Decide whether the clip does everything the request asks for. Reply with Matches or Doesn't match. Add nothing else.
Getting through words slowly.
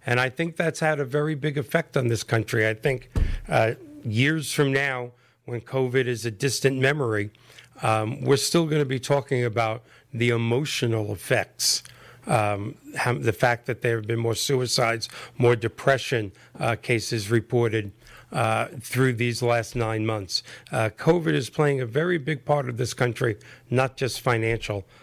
Doesn't match